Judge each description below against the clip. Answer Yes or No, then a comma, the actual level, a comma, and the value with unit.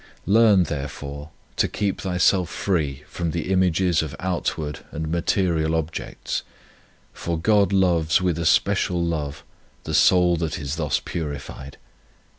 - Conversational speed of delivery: No, slow, 130 wpm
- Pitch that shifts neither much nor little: Yes, average, 3.3 semitones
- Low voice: Yes, very low, 85 Hz